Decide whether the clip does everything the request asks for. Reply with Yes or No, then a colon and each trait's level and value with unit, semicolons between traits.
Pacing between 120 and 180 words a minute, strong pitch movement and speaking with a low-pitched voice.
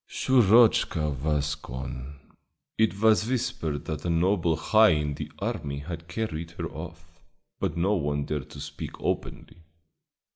Yes: average, 140 wpm; wide, 5.8 semitones; very low, 80 Hz